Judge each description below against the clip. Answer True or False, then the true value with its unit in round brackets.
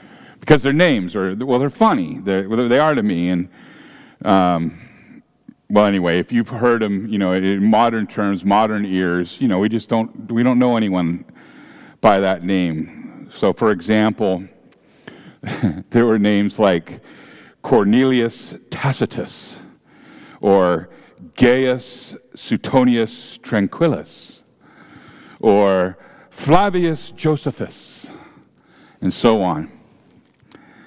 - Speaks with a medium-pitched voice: False (110 Hz)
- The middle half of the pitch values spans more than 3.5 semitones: True (4.9 semitones)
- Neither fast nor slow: False (115 wpm)